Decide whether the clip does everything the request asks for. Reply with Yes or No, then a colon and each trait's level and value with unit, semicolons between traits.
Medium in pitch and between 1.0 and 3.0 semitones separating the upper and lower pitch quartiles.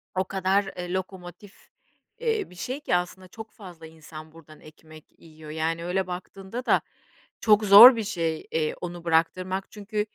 No: medium, 180 Hz; average, 3.6 semitones